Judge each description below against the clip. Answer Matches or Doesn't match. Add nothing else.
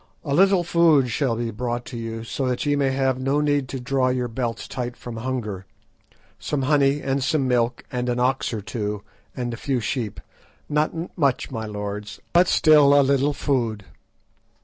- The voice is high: Doesn't match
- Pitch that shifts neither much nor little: Matches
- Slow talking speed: Doesn't match